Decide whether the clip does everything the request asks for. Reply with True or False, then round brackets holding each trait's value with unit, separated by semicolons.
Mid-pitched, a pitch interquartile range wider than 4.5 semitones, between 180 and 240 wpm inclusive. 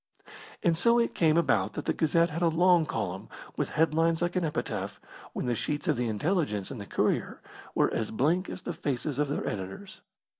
True (155 Hz; 5.5 semitones; 200 wpm)